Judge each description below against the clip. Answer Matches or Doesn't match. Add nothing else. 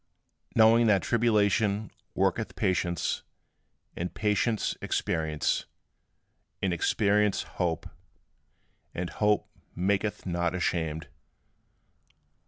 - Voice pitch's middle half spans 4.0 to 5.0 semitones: Doesn't match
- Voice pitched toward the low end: Matches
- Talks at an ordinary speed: Doesn't match